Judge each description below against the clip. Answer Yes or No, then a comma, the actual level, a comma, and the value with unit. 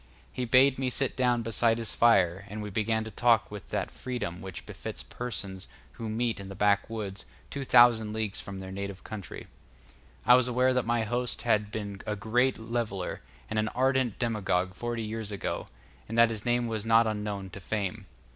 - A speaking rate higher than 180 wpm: Yes, average, 190 wpm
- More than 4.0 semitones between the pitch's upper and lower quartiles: No, average, 3.0 semitones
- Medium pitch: No, low, 110 Hz